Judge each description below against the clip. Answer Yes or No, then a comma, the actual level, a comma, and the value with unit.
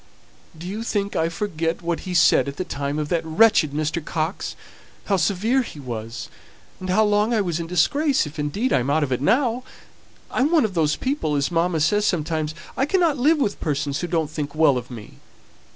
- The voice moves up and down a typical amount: No, wide, 5.8 semitones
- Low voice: No, medium, 170 Hz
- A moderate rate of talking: No, fast, 210 wpm